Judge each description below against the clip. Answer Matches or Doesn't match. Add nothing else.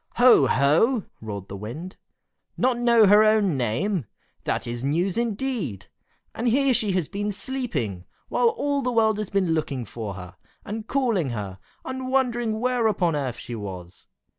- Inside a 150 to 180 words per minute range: Matches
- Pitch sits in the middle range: Doesn't match